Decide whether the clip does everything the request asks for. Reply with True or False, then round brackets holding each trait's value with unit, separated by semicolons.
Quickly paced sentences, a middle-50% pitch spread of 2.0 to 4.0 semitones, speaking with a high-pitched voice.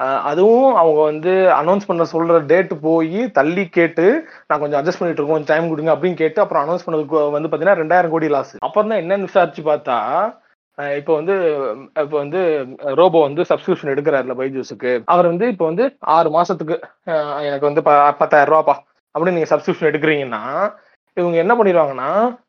False (160 wpm; 3.4 semitones; 165 Hz)